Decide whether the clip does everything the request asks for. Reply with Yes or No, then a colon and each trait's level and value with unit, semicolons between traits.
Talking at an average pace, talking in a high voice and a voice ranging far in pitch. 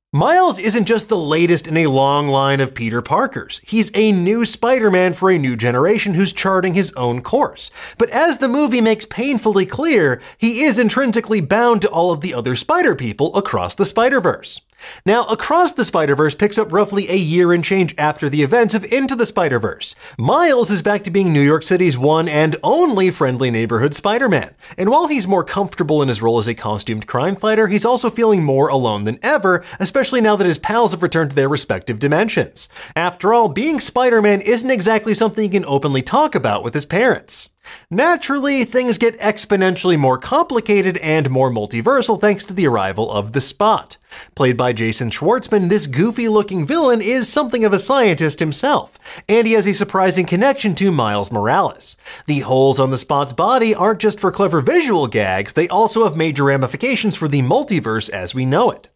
Yes: average, 190 wpm; high, 195 Hz; wide, 7.4 semitones